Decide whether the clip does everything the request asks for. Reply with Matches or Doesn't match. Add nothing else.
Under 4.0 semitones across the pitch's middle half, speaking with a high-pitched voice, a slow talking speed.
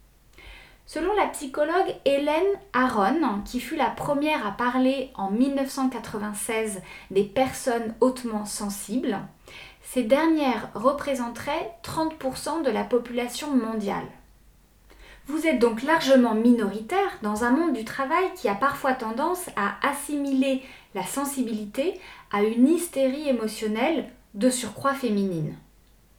Doesn't match